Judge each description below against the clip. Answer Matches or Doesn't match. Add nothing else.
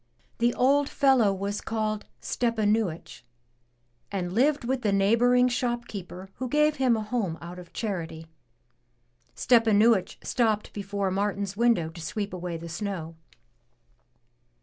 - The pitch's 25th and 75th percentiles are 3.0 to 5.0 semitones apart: Matches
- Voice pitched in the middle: Doesn't match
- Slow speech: Matches